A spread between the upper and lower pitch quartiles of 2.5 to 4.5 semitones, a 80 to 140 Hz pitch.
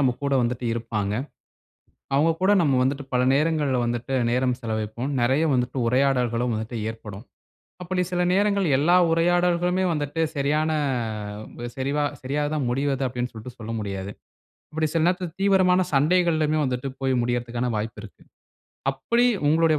No: average, 5.1 semitones; low, 135 Hz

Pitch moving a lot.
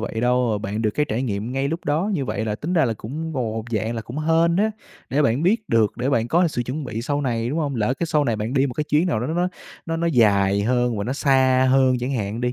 No: average, 5.0 semitones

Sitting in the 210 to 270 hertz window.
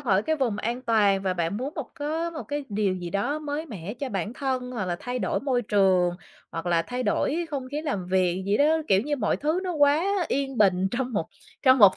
Yes: high, 240 Hz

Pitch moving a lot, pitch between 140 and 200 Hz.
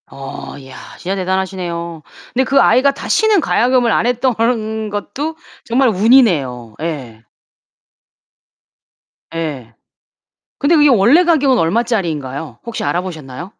Yes: wide, 8.3 semitones; high, 195 Hz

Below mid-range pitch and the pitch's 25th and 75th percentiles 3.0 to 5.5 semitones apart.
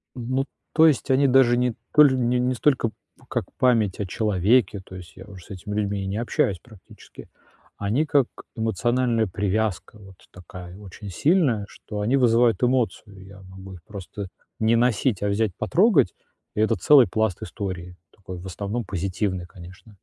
Yes: low, 105 Hz; average, 4.3 semitones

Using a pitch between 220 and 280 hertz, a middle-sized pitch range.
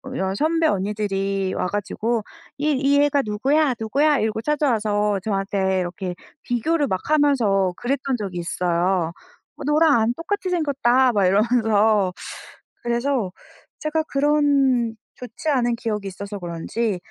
No: high, 230 Hz; wide, 6.2 semitones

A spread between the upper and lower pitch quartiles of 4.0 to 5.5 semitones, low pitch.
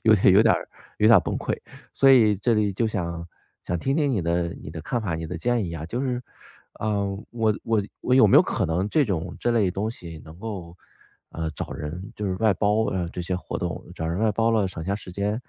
Yes: average, 4.5 semitones; low, 100 Hz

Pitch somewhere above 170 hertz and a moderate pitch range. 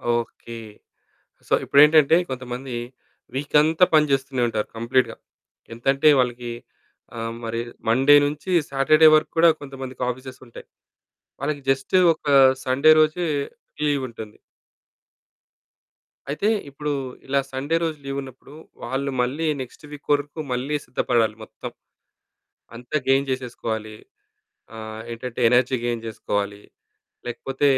No: low, 135 Hz; average, 3.2 semitones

